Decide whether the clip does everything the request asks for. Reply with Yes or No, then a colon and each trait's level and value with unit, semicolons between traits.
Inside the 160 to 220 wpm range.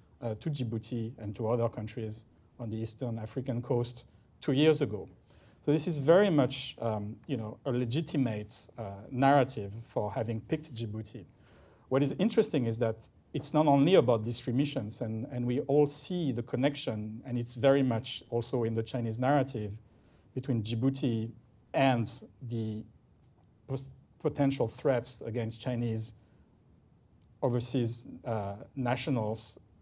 No: average, 145 wpm